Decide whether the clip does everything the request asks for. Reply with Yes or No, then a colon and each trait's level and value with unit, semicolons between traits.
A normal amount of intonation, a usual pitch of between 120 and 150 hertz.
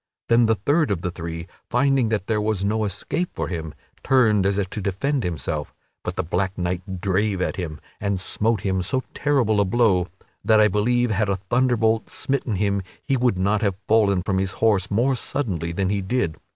No: average, 3.7 semitones; low, 100 Hz